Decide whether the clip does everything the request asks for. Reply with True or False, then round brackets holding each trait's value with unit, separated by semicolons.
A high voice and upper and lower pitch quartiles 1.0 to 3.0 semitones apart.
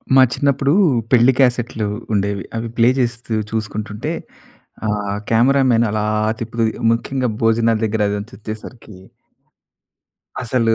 False (115 Hz; 2.4 semitones)